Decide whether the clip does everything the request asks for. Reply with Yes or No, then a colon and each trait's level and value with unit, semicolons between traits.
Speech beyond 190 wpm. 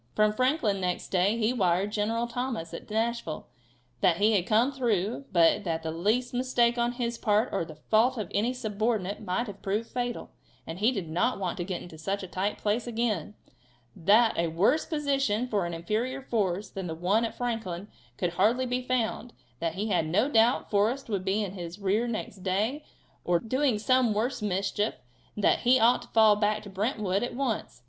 Yes: average, 200 wpm